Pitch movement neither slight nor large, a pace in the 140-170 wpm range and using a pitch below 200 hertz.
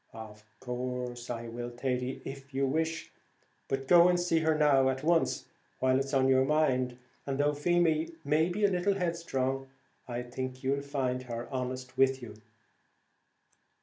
Yes: average, 3.6 semitones; average, 165 wpm; low, 135 Hz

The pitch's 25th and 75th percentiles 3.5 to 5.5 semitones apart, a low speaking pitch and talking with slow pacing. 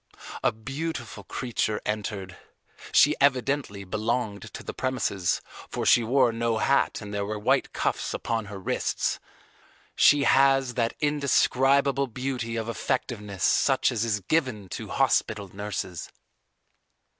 Yes: average, 4.4 semitones; low, 115 Hz; slow, 130 wpm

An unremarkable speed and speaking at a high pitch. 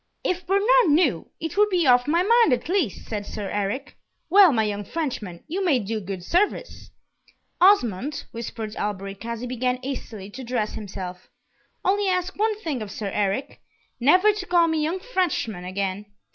Yes: average, 170 wpm; very high, 260 Hz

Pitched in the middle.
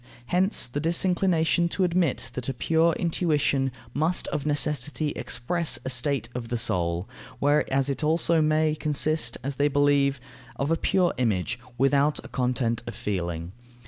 Yes: medium, 145 Hz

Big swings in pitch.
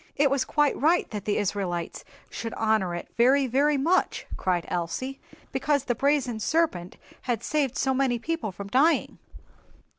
Yes: wide, 5.7 semitones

